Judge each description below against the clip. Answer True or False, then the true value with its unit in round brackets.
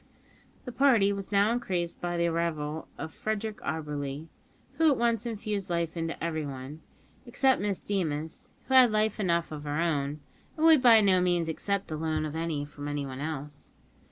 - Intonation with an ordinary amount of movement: False (5.7 semitones)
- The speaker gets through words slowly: False (175 wpm)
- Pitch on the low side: False (170 Hz)